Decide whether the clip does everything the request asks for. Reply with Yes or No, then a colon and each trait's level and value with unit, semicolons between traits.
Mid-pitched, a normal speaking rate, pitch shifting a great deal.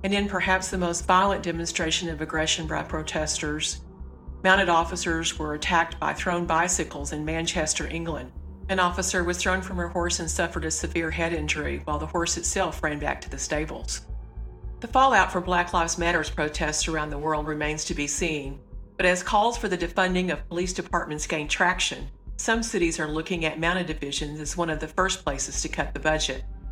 No: medium, 165 Hz; average, 190 wpm; average, 3.2 semitones